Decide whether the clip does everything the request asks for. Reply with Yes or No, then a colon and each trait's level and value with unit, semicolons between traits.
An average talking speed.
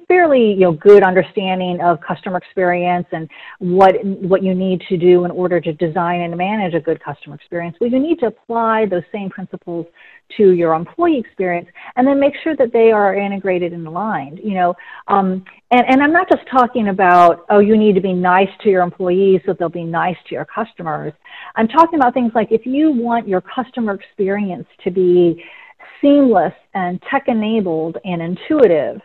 Yes: average, 190 wpm